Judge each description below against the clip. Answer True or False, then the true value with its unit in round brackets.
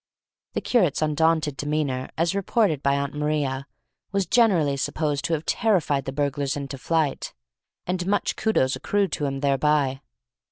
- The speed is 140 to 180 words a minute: True (150 wpm)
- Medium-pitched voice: True (150 Hz)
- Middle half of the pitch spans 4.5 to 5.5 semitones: False (3.8 semitones)